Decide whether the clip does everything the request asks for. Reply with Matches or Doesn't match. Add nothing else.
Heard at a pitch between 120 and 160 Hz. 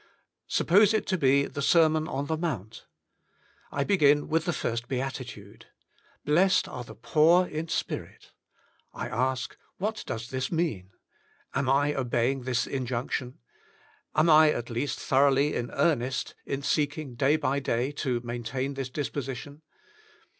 Matches